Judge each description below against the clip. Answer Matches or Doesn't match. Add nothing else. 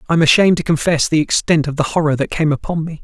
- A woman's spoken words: Doesn't match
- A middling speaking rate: Doesn't match